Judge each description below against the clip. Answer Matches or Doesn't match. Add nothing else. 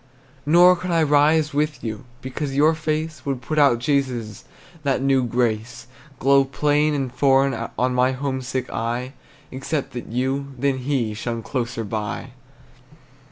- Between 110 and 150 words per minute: Matches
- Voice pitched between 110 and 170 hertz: Matches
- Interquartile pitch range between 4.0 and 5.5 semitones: Doesn't match